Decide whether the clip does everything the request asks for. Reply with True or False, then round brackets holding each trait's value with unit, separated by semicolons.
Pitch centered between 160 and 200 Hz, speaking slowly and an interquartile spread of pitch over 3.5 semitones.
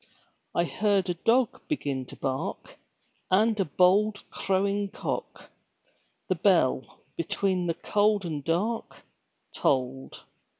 True (190 Hz; 115 wpm; 4.1 semitones)